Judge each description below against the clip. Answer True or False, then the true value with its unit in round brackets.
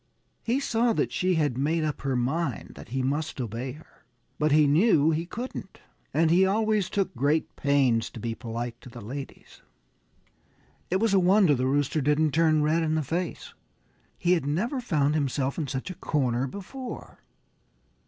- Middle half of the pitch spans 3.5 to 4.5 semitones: False (5.1 semitones)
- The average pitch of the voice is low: False (155 Hz)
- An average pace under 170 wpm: False (175 wpm)